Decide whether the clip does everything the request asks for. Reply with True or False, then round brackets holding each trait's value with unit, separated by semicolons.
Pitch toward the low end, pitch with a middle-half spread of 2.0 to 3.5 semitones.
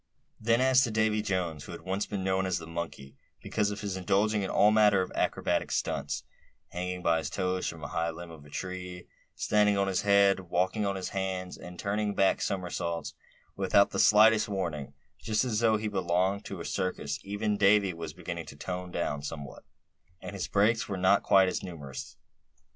True (95 Hz; 3.1 semitones)